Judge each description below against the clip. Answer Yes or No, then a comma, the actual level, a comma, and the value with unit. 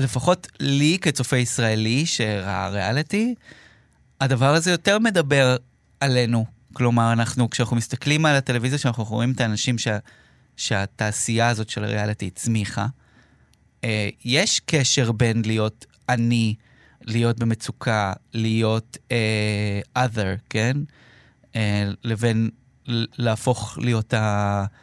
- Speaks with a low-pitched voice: Yes, low, 120 Hz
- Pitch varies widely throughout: No, average, 2.9 semitones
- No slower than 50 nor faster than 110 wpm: Yes, average, 105 wpm